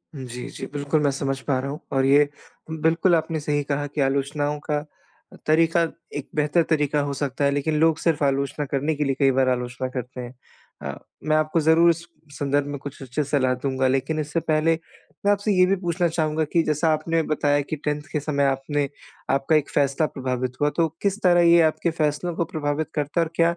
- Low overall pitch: No, medium, 145 Hz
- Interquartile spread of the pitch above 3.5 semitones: No, narrow, 2.6 semitones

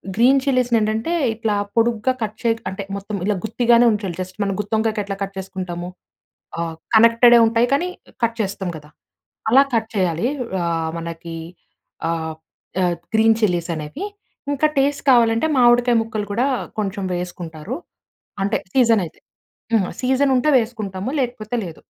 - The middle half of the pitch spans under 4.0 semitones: No, average, 4.3 semitones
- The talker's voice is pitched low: No, high, 220 Hz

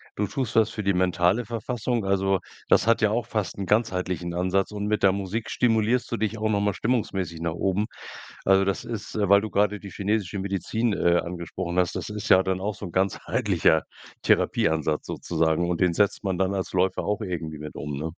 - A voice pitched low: Yes, very low, 95 Hz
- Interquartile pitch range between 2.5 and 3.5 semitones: Yes, average, 2.9 semitones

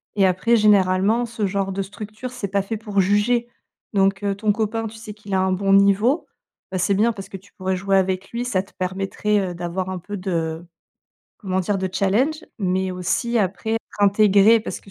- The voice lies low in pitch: No, high, 200 Hz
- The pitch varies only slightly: Yes, narrow, 2.2 semitones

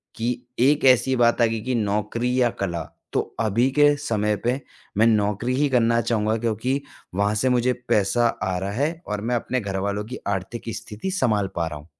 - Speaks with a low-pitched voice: Yes, low, 115 Hz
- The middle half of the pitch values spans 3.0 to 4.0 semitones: Yes, average, 3.4 semitones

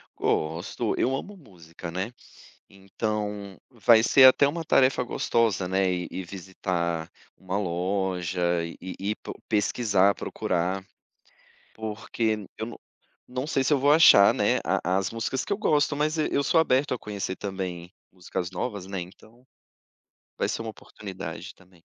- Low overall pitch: Yes, low, 100 Hz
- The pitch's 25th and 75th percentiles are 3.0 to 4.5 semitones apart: No, average, 5.0 semitones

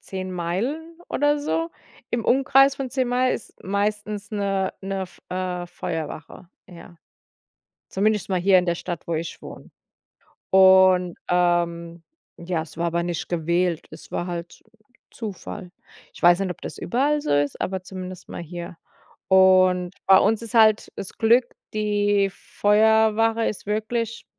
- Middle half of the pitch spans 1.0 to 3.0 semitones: No, average, 3.9 semitones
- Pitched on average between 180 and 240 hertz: Yes, high, 190 Hz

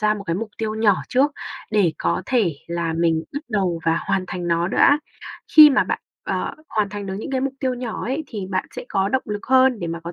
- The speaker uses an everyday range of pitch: No, wide, 6.6 semitones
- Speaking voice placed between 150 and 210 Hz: Yes, high, 205 Hz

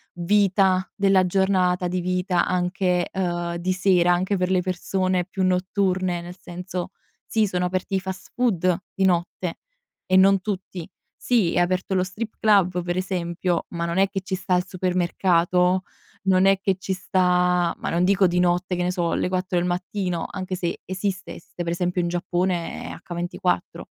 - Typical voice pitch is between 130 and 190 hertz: Yes, medium, 185 Hz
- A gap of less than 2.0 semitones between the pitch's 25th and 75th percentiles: Yes, narrow, 1.2 semitones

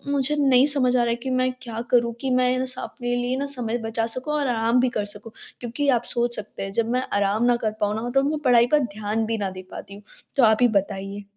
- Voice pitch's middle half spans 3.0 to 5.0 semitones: No, narrow, 2.6 semitones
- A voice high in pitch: Yes, high, 240 Hz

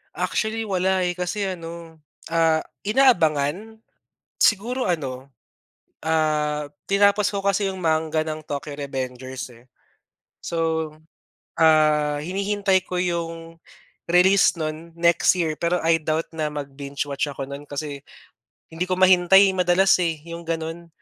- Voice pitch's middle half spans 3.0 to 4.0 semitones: Yes, average, 3.4 semitones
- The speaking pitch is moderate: Yes, medium, 165 Hz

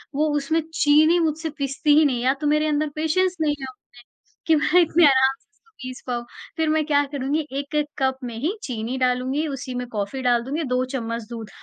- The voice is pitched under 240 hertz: No, very high, 280 Hz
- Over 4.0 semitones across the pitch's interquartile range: No, average, 3.5 semitones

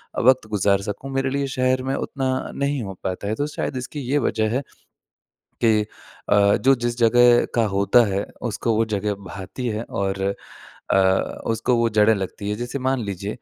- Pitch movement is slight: No, average, 4.2 semitones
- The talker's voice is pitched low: Yes, low, 115 Hz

